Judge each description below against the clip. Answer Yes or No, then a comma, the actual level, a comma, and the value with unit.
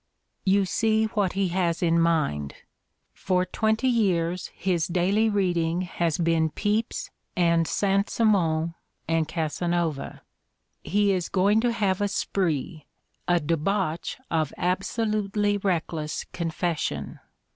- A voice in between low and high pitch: Yes, medium, 180 Hz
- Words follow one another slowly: Yes, slow, 125 wpm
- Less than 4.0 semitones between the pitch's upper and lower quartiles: Yes, average, 3.5 semitones